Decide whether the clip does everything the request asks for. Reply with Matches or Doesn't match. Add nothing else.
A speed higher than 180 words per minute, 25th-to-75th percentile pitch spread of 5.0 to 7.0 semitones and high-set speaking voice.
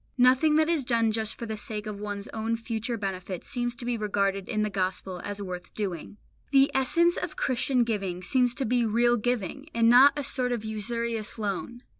Doesn't match